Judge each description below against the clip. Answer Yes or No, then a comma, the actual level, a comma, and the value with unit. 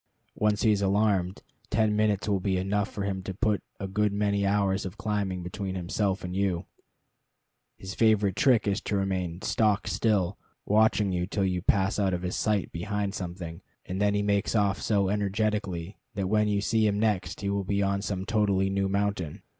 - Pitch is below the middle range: Yes, low, 100 Hz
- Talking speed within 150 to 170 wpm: No, average, 195 wpm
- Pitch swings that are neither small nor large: No, narrow, 1.7 semitones